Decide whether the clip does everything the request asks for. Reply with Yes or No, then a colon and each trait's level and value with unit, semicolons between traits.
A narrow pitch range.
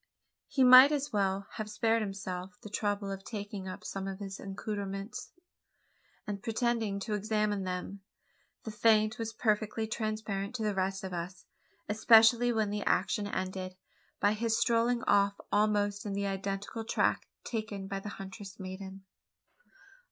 Yes: narrow, 2.1 semitones